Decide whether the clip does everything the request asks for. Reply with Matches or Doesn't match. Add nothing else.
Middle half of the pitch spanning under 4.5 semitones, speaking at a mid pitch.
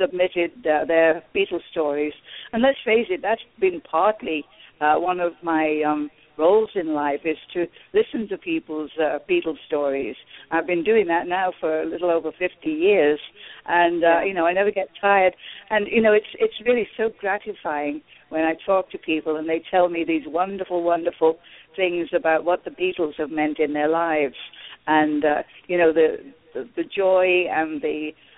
Matches